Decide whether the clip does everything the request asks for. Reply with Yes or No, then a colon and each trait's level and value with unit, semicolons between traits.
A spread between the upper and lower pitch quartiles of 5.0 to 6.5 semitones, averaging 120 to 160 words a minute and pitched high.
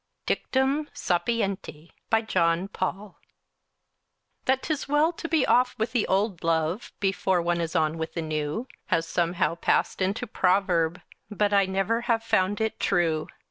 Yes: average, 5.3 semitones; average, 155 wpm; high, 195 Hz